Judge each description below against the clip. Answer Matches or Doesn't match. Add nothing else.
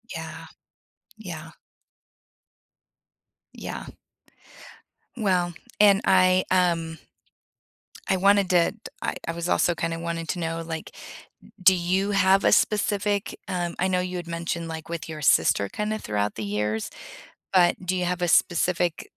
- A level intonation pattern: Matches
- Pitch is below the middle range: Doesn't match